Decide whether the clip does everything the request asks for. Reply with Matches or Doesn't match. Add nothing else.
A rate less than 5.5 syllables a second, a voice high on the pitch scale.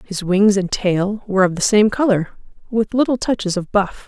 Matches